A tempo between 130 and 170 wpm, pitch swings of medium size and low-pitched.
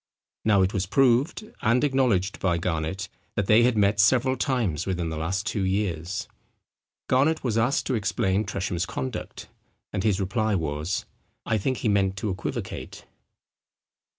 Yes: average, 150 wpm; average, 4.1 semitones; low, 100 Hz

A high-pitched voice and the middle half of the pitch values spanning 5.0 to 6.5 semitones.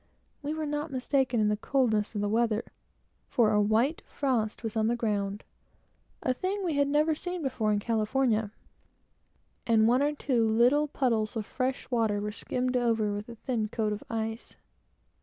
No: high, 235 Hz; average, 3.8 semitones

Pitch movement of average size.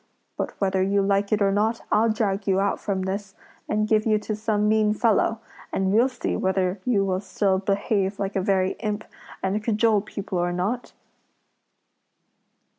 No: narrow, 1.9 semitones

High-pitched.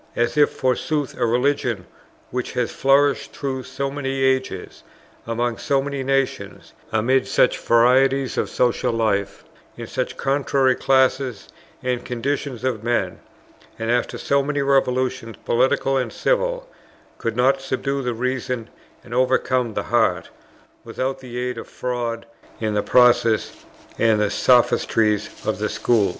No: low, 125 Hz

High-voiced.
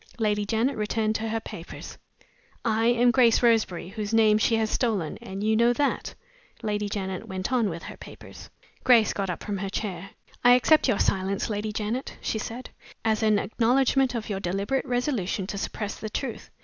Yes: high, 220 Hz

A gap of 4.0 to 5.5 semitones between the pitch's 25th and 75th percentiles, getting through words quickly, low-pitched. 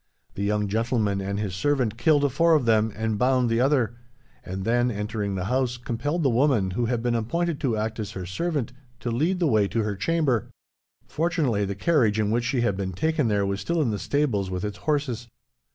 Yes: average, 5.2 semitones; fast, 215 wpm; low, 115 Hz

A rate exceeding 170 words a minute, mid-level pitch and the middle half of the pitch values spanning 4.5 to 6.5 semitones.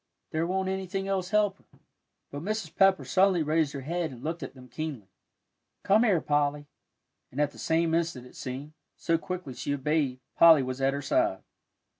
Yes: average, 185 wpm; medium, 160 Hz; average, 4.9 semitones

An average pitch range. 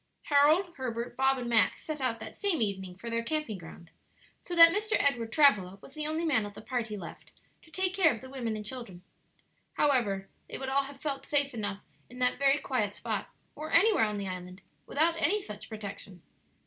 No: wide, 6.3 semitones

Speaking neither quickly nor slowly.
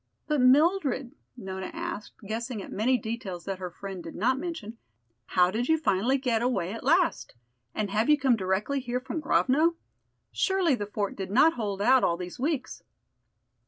Yes: average, 175 wpm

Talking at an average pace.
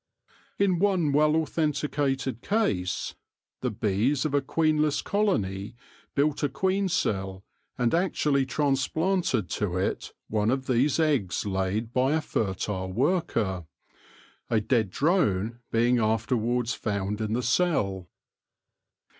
No: slow, 125 wpm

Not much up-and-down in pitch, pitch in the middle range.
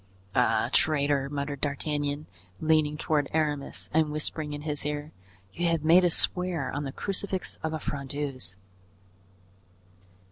Yes: narrow, 1.8 semitones; medium, 150 Hz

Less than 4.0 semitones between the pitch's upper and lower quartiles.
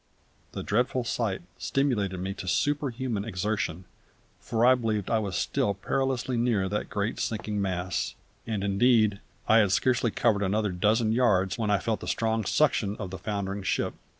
Yes: average, 3.2 semitones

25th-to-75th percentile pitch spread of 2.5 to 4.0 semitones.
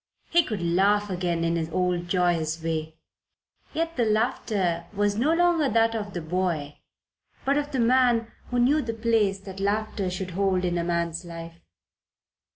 No: average, 5.1 semitones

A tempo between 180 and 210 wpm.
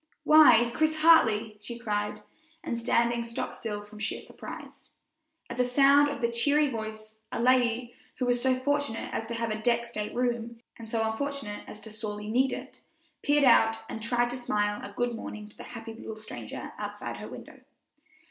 Yes: average, 185 wpm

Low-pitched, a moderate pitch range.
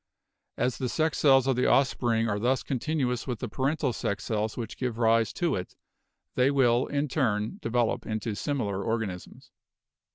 Yes: low, 120 Hz; average, 3.3 semitones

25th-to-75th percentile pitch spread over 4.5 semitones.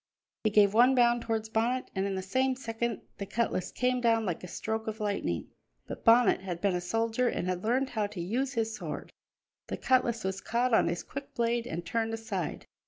No: average, 3.5 semitones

